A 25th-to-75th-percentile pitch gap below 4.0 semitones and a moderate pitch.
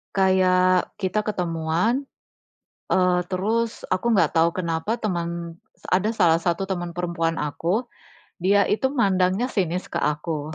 Yes: average, 2.8 semitones; medium, 180 Hz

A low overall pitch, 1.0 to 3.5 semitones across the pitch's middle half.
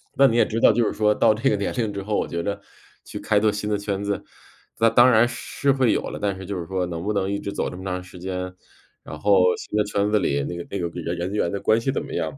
Yes: low, 100 Hz; average, 2.8 semitones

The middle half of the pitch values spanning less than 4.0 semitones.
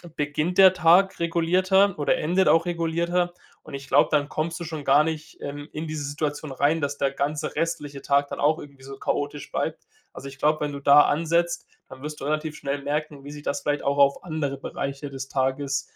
Yes: average, 2.7 semitones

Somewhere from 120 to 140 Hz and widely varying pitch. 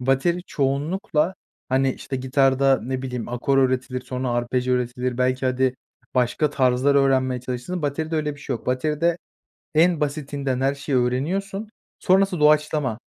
No: low, 135 Hz; average, 2.9 semitones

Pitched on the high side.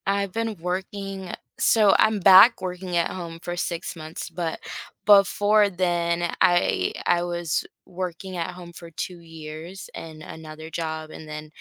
No: medium, 175 Hz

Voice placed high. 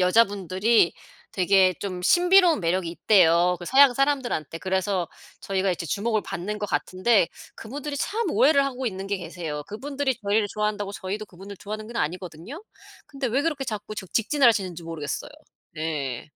Yes: high, 200 Hz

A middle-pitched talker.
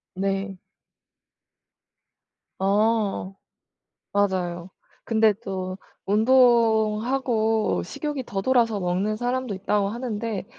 No: high, 215 Hz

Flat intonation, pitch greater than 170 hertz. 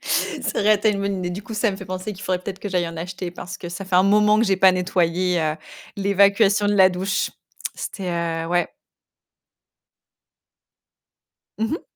Yes: narrow, 2.1 semitones; high, 190 Hz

